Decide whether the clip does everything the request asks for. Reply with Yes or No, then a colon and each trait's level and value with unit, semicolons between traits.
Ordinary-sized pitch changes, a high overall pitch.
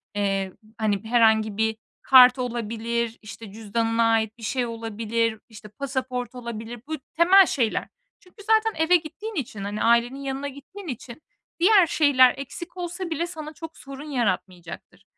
No: wide, 5.7 semitones; high, 240 Hz